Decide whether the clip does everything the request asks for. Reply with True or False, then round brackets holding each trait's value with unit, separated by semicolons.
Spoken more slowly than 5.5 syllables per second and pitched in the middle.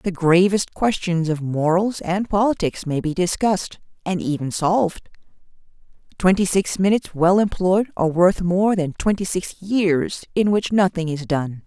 True (4.5 syllables/s; 180 Hz)